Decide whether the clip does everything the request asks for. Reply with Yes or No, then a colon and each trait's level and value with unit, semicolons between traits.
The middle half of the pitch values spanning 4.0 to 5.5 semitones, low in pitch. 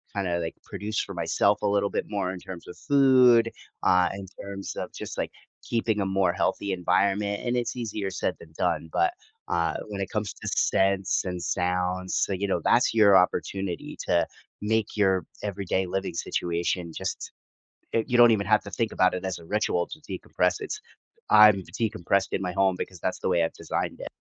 No: average, 2.7 semitones; low, 100 Hz